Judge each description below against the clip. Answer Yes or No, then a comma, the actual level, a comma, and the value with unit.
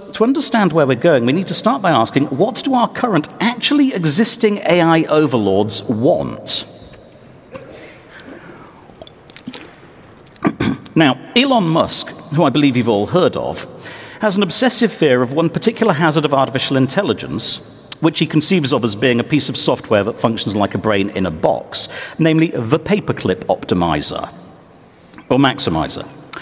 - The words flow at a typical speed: Yes, average, 150 wpm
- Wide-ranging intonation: Yes, wide, 8.4 semitones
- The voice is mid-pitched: Yes, medium, 160 Hz